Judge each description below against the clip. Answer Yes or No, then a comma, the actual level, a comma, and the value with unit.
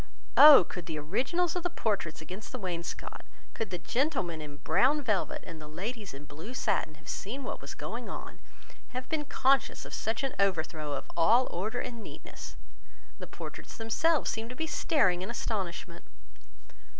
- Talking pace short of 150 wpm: No, average, 175 wpm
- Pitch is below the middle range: No, high, 210 Hz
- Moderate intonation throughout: No, wide, 7.5 semitones